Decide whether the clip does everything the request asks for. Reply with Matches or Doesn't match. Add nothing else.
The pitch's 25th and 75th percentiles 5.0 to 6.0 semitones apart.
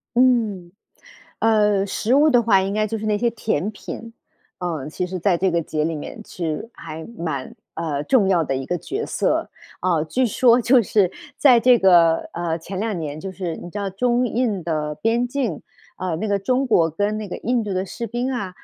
Matches